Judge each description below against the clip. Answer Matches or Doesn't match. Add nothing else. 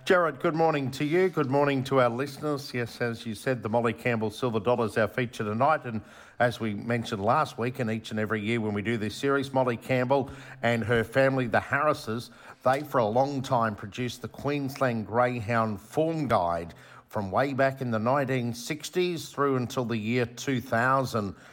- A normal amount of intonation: Matches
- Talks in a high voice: Doesn't match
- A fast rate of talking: Doesn't match